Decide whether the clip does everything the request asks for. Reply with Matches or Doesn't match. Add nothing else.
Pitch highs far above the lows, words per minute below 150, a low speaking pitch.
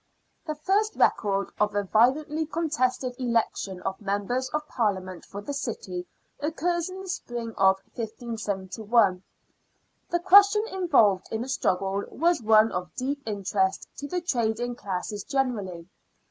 Doesn't match